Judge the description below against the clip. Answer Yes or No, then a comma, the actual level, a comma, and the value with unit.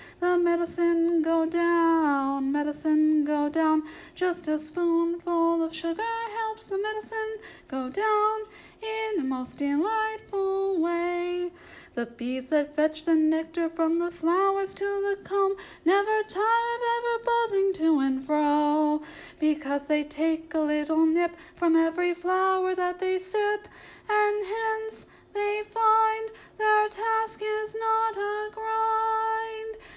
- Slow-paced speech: Yes, slow, 130 wpm